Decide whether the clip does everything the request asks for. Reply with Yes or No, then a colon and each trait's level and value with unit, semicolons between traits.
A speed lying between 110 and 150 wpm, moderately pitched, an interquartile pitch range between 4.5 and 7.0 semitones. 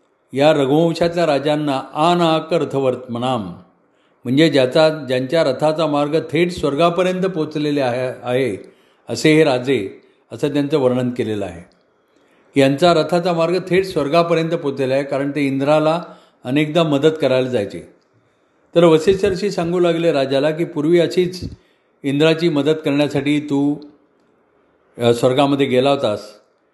No: average, 115 wpm; medium, 145 Hz; average, 3.7 semitones